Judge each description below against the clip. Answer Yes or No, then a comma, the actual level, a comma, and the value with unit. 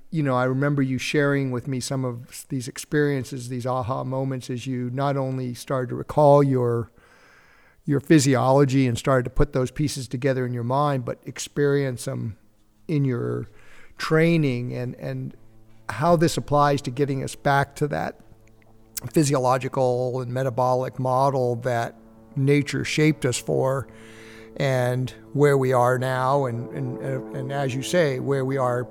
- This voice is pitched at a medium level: No, low, 130 Hz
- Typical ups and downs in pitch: No, narrow, 2.2 semitones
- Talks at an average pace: Yes, average, 155 wpm